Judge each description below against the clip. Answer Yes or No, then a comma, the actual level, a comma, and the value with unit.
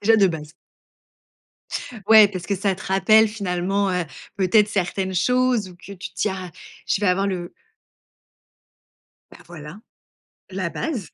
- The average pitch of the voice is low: No, high, 195 Hz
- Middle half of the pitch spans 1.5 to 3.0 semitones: Yes, average, 2.7 semitones